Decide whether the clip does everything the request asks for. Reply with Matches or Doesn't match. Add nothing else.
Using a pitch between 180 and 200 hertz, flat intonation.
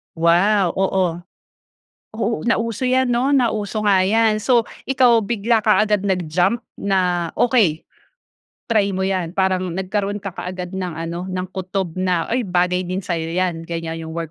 Doesn't match